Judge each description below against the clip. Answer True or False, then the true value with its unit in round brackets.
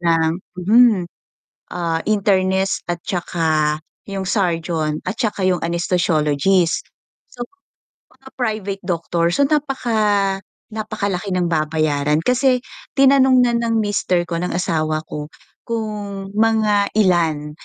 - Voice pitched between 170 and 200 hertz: True (190 Hz)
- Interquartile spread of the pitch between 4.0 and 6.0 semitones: True (4.7 semitones)